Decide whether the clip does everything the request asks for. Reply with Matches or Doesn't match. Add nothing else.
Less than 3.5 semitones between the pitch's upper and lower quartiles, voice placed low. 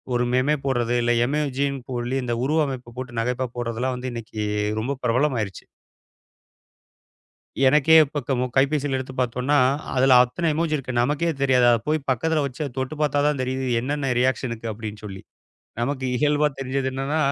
Matches